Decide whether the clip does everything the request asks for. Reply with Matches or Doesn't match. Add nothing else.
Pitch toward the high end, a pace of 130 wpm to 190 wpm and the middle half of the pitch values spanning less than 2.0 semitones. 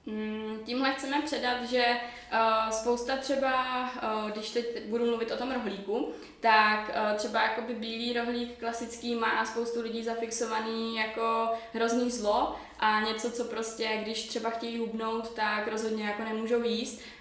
Matches